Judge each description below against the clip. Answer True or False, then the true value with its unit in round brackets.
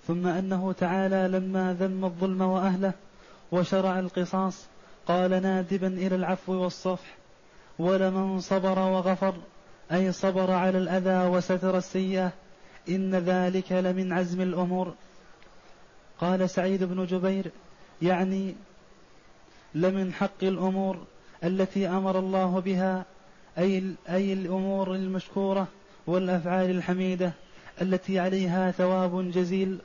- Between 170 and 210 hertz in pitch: True (185 Hz)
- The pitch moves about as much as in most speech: False (0.7 semitones)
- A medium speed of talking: True (100 wpm)